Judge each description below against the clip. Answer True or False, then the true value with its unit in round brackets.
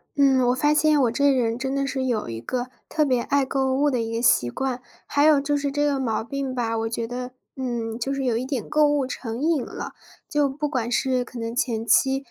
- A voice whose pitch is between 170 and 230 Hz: False (260 Hz)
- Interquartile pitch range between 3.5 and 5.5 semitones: False (2.9 semitones)